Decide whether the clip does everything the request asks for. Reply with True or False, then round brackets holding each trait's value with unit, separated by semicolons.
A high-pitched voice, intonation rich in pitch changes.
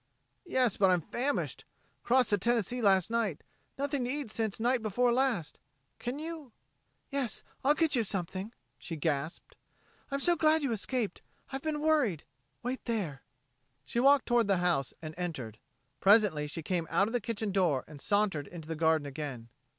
True (215 Hz; 7.3 semitones)